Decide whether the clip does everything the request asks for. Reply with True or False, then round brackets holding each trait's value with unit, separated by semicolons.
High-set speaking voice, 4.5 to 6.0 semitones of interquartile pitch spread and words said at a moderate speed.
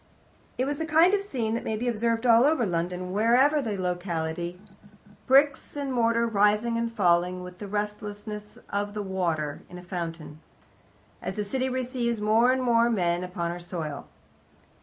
True (210 Hz; 4.9 semitones; 170 wpm)